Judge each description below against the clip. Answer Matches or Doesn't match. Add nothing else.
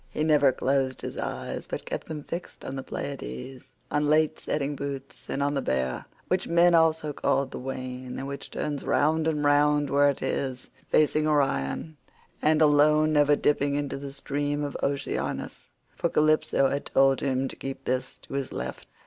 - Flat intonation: Matches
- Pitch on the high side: Doesn't match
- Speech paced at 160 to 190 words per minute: Matches